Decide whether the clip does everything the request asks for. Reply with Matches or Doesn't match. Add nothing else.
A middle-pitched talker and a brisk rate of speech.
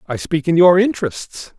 Doesn't match